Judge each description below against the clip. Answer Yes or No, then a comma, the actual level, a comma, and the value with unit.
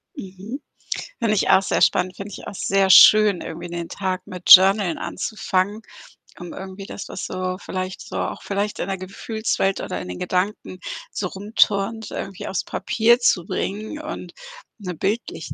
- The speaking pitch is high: Yes, high, 195 Hz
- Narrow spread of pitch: Yes, narrow, 2.3 semitones